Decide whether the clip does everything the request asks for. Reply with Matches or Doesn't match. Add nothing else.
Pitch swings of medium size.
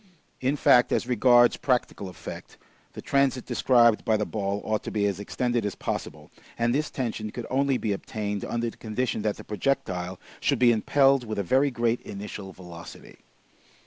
Matches